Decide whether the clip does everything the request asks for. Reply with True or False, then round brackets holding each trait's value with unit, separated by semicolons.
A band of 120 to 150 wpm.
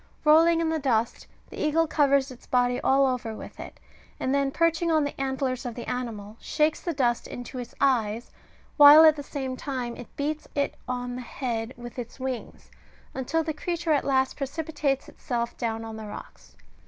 False (185 wpm)